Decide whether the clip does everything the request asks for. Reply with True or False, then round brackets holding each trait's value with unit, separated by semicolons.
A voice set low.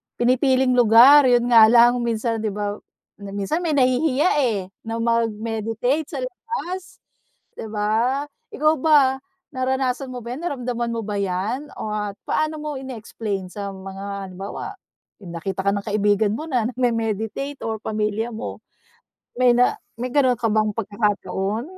False (230 Hz)